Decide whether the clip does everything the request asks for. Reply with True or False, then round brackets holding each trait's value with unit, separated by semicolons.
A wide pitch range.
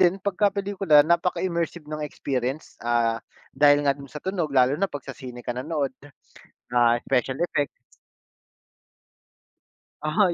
False (5.0 semitones)